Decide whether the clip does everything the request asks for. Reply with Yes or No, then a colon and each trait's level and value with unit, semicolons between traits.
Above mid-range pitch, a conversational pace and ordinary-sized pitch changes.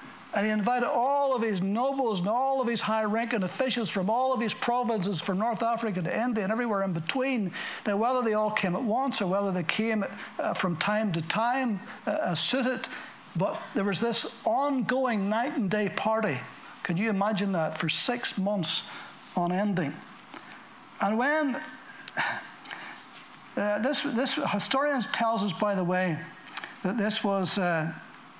Yes: high, 215 Hz; average, 165 wpm; average, 4.0 semitones